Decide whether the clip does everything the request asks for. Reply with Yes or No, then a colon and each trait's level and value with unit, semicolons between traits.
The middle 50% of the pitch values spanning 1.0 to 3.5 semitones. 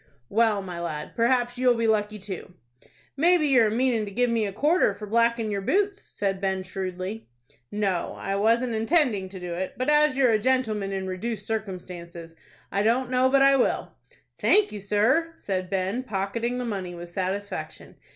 No: average, 4.5 semitones